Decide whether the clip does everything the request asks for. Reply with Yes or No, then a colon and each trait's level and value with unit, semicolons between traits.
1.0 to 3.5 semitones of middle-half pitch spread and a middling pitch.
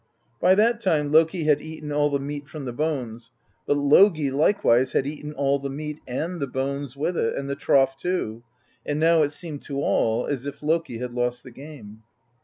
Yes: narrow, 2.6 semitones; medium, 145 Hz